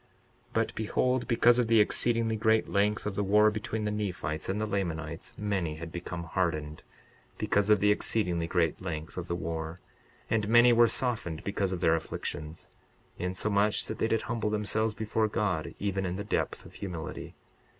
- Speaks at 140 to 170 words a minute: No, average, 180 wpm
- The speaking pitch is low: Yes, low, 100 Hz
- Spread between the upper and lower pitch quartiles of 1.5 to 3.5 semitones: No, average, 4.1 semitones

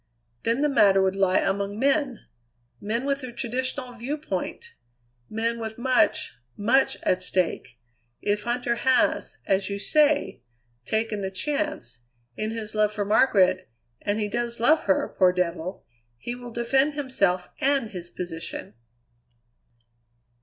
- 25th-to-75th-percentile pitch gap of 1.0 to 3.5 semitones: No, average, 5.1 semitones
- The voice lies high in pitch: Yes, high, 225 Hz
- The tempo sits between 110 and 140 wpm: Yes, slow, 135 wpm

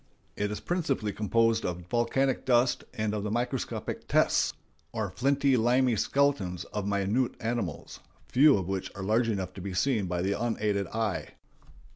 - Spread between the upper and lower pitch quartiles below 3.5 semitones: No, average, 3.9 semitones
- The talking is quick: No, average, 160 wpm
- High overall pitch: No, low, 110 Hz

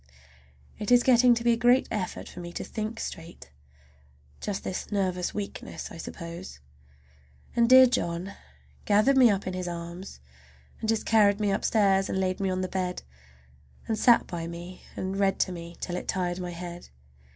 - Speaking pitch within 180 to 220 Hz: Yes, high, 190 Hz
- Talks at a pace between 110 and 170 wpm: No, average, 180 wpm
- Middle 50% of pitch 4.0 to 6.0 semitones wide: No, average, 3.6 semitones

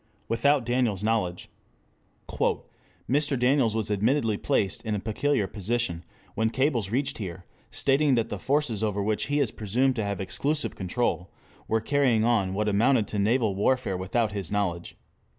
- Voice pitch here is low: Yes, low, 110 Hz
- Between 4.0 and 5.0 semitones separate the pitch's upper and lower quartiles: Yes, average, 4.4 semitones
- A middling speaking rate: Yes, average, 155 wpm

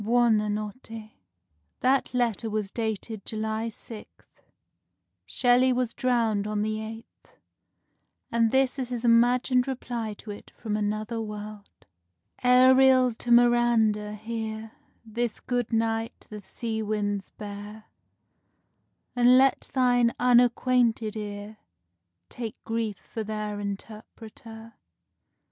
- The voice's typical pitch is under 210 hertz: No, high, 225 Hz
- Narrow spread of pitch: Yes, narrow, 2.3 semitones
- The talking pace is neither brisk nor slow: No, slow, 110 wpm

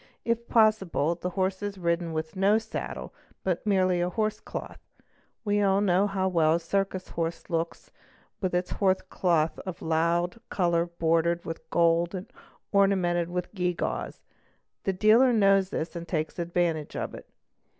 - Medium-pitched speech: Yes, medium, 180 Hz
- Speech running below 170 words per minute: Yes, average, 160 wpm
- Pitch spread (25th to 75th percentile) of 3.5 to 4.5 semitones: No, average, 2.7 semitones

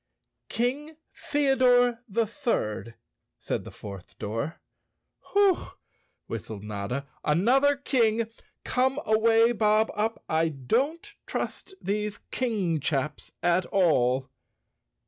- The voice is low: No, high, 220 Hz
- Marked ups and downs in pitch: Yes, wide, 9.0 semitones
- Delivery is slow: Yes, slow, 100 wpm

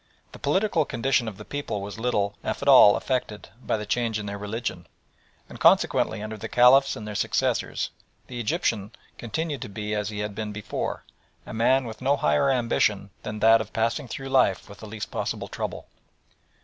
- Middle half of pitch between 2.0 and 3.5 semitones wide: Yes, average, 3.1 semitones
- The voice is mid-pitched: No, low, 110 Hz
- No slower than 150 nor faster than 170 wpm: No, average, 190 wpm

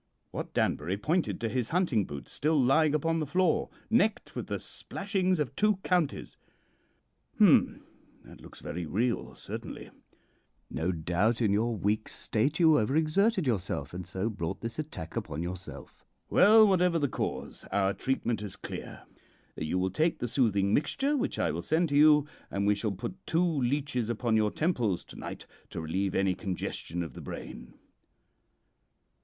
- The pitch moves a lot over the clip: Yes, wide, 8.5 semitones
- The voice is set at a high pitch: No, low, 120 Hz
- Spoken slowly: No, average, 165 wpm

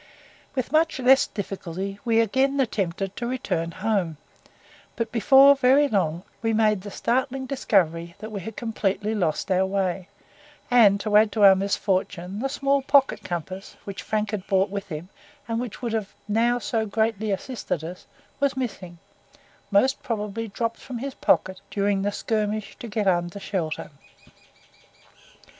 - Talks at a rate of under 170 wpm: Yes, average, 155 wpm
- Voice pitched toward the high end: Yes, high, 210 Hz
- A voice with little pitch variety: No, average, 3.8 semitones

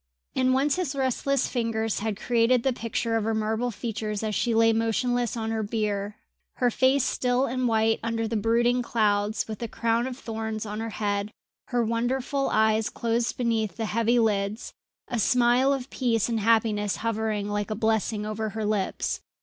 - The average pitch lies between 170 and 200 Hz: No, high, 225 Hz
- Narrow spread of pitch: Yes, narrow, 2.1 semitones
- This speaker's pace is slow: No, average, 180 wpm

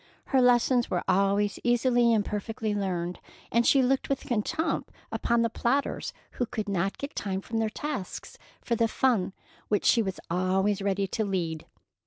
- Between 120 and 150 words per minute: No, average, 170 wpm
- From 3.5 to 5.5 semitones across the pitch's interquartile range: Yes, average, 3.8 semitones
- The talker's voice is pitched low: No, high, 215 Hz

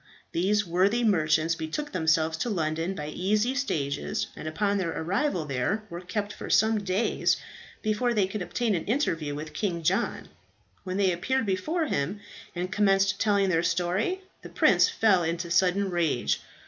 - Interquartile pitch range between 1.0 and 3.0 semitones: No, average, 4.3 semitones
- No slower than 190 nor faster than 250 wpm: No, average, 160 wpm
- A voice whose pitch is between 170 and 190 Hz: Yes, medium, 185 Hz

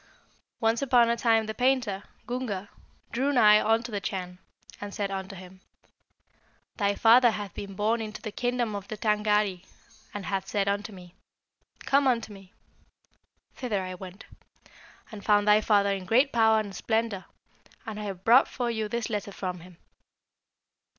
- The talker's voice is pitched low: No, high, 210 Hz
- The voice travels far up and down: No, average, 2.8 semitones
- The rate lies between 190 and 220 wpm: No, average, 165 wpm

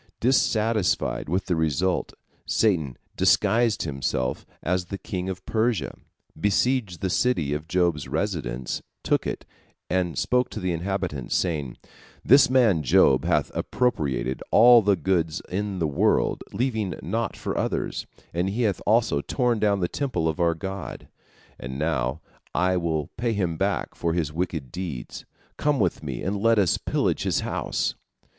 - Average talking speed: Yes, average, 155 wpm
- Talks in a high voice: No, very low, 90 Hz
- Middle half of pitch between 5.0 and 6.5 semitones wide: Yes, average, 5.3 semitones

